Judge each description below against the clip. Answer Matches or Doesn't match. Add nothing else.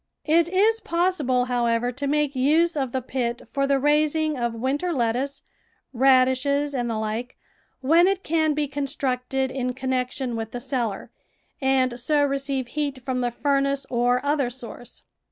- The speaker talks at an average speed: Matches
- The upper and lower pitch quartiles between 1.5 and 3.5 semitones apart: Matches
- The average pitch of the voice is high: Matches